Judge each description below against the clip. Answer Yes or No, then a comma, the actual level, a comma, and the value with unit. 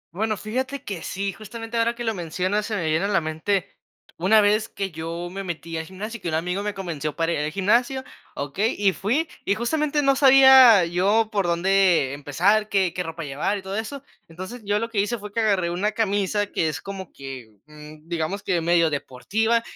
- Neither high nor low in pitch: No, high, 195 Hz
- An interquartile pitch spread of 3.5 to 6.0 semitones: Yes, average, 4.6 semitones